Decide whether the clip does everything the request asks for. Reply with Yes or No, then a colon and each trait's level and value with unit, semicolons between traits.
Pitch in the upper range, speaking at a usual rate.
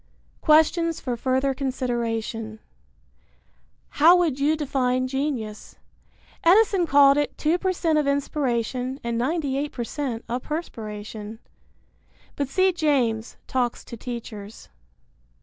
No: very high, 265 Hz; slow, 95 wpm